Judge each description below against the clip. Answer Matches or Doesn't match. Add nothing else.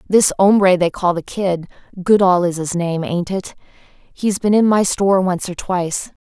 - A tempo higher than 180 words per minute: Doesn't match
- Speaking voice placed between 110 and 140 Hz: Doesn't match